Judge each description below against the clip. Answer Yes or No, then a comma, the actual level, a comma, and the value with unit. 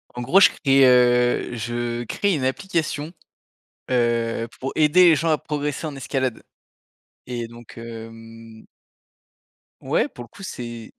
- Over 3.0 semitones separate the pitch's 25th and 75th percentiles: Yes, average, 4.0 semitones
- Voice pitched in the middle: No, low, 125 Hz